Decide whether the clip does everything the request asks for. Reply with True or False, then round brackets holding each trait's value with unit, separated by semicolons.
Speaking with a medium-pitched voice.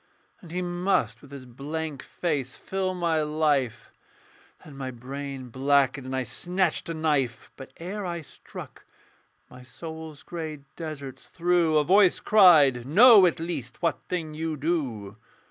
True (155 Hz)